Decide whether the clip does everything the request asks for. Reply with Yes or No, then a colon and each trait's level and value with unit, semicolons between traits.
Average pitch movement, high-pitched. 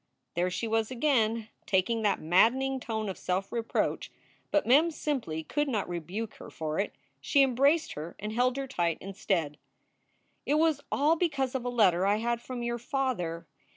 No: wide, 6.0 semitones; high, 230 Hz